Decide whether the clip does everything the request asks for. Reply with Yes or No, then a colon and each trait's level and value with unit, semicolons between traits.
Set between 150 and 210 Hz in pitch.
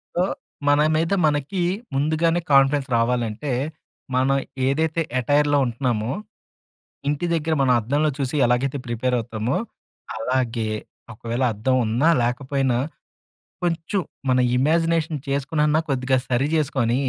No: low, 135 Hz